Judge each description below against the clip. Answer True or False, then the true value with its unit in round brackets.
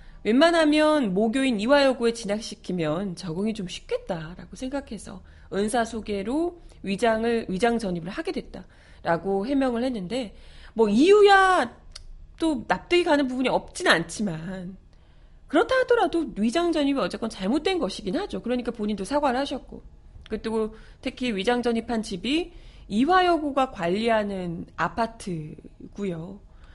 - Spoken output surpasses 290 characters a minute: True (305 characters per minute)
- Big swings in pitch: True (6.4 semitones)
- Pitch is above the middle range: True (230 Hz)